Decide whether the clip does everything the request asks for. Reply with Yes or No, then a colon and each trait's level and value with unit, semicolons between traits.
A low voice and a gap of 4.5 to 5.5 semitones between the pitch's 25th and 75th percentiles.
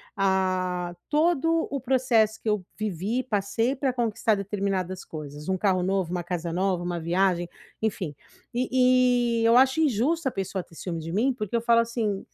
No: high, 205 Hz; average, 5.1 semitones